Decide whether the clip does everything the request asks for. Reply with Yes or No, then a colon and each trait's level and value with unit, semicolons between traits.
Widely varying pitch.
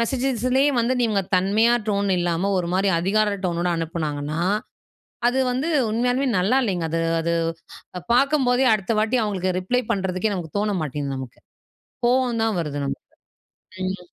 Yes: wide, 5.7 semitones